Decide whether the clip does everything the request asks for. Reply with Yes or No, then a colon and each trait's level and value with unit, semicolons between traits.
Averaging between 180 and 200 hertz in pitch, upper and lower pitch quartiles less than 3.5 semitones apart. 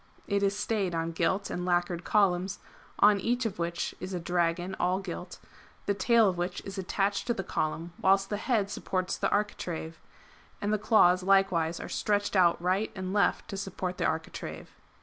Yes: high, 190 Hz; narrow, 2.4 semitones